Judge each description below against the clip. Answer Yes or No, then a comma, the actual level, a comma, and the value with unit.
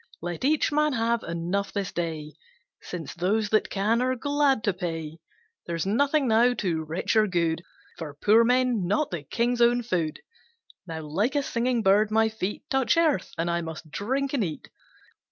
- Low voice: No, high, 210 Hz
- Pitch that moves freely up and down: Yes, wide, 6.4 semitones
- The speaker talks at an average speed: Yes, average, 175 wpm